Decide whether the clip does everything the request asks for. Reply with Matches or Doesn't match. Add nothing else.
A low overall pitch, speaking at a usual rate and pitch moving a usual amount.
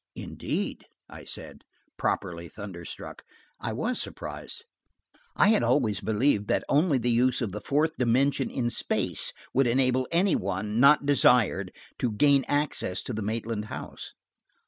Matches